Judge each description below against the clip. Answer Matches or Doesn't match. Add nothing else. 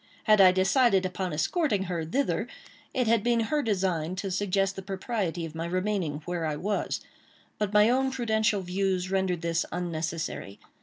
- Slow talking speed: Doesn't match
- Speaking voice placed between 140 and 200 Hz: Matches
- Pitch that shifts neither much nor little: Matches